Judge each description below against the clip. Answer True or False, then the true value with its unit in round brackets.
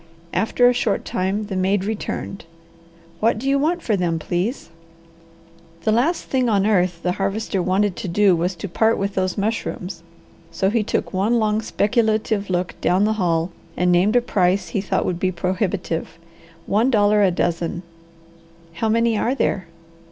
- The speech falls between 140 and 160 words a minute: False (170 wpm)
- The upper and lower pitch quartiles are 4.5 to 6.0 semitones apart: False (3.4 semitones)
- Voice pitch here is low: False (200 Hz)